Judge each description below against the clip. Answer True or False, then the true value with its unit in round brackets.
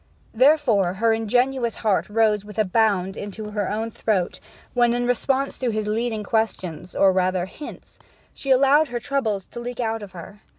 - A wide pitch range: False (3.2 semitones)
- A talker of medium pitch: False (220 Hz)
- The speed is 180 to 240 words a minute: False (170 wpm)